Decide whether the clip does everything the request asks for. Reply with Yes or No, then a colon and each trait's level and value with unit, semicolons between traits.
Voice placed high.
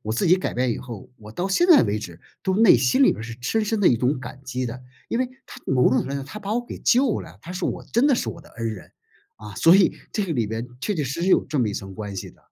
No: low, 135 Hz